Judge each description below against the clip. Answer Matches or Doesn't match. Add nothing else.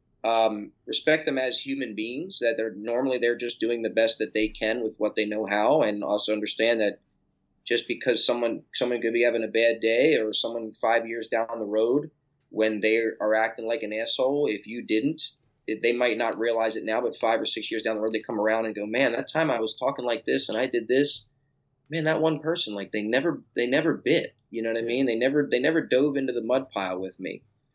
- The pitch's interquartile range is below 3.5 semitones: Matches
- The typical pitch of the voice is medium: Doesn't match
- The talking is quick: Matches